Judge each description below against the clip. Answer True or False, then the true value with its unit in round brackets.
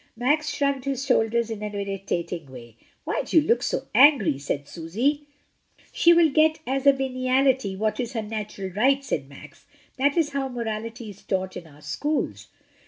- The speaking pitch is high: True (235 Hz)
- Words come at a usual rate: True (175 wpm)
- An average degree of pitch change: False (6.2 semitones)